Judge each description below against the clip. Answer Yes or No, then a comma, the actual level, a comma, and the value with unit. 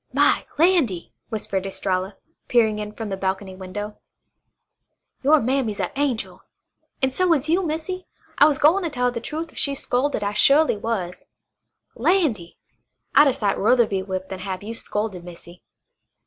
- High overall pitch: Yes, high, 225 Hz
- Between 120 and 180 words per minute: Yes, average, 160 wpm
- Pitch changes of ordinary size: No, wide, 6.9 semitones